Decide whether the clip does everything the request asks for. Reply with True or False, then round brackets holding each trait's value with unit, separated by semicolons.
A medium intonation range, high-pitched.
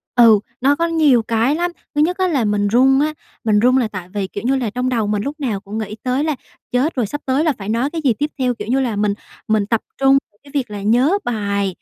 True (4.9 semitones; 245 Hz)